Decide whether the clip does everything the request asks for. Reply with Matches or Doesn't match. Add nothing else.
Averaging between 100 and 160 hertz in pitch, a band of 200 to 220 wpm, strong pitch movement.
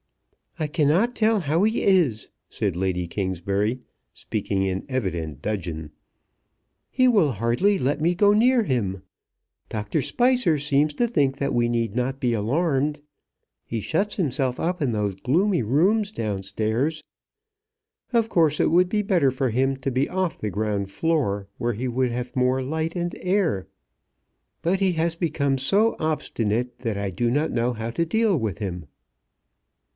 Doesn't match